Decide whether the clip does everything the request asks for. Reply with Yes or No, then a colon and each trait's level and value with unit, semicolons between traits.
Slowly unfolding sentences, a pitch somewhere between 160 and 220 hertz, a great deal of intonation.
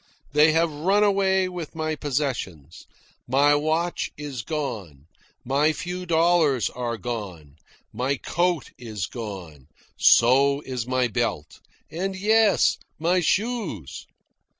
No: slow, 115 wpm; medium, 145 Hz; wide, 6.6 semitones